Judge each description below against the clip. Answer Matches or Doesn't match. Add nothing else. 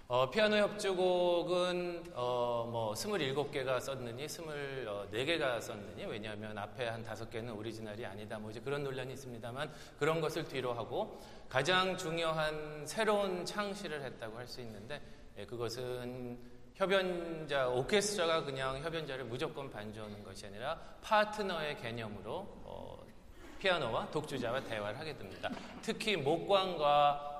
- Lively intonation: Matches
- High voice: Doesn't match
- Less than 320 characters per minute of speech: Matches